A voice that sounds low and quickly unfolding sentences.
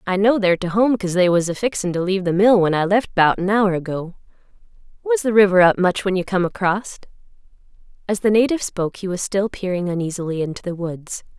No: medium, 185 Hz; fast, 220 wpm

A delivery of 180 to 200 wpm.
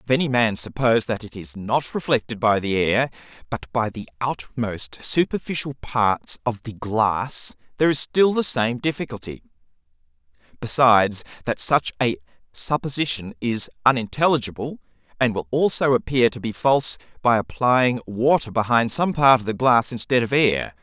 No: average, 155 wpm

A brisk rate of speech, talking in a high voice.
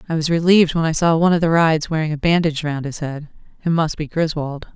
No: fast, 255 wpm; medium, 160 Hz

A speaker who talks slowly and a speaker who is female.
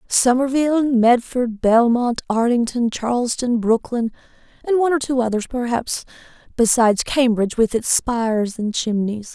Yes: slow, 120 wpm; female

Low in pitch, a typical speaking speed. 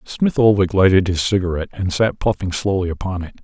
Yes: very low, 95 Hz; average, 190 wpm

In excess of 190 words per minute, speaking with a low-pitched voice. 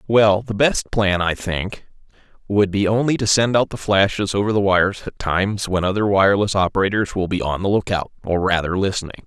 Yes: average, 200 wpm; low, 100 Hz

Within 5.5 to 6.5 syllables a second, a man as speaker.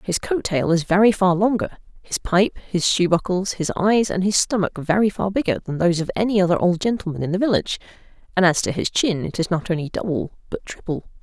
No: 6.0 syllables/s; female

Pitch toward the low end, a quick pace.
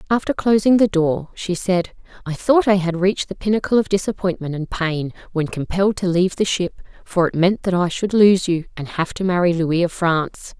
No: medium, 185 Hz; fast, 215 wpm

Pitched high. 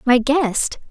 Yes: very high, 260 Hz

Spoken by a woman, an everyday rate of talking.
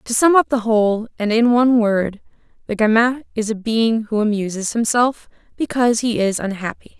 Yes: female; average, 180 wpm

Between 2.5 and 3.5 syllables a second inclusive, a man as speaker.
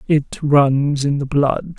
No: 3.1 syllables/s; female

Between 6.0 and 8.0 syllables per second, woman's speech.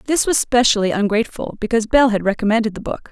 Yes: 6.9 syllables/s; female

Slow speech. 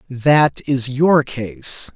Yes: slow, 125 wpm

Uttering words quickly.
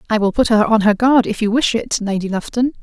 Yes: fast, 275 wpm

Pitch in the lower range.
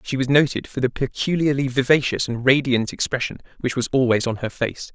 Yes: low, 130 Hz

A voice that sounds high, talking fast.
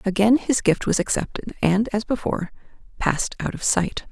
No: high, 210 Hz; average, 175 wpm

